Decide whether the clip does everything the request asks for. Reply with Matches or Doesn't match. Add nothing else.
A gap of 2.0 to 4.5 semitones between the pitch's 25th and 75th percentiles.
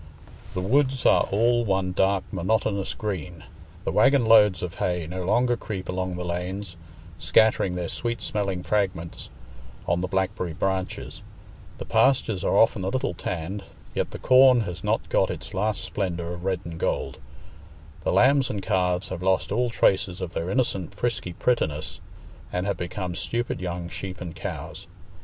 Matches